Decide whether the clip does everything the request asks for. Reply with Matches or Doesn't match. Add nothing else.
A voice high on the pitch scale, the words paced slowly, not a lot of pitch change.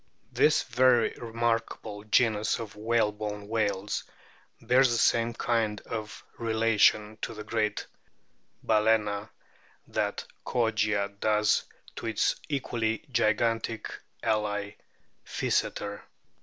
Doesn't match